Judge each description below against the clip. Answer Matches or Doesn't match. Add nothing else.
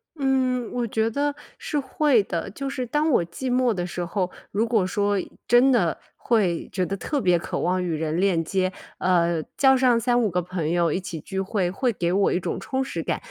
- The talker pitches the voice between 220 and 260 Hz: Doesn't match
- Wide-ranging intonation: Matches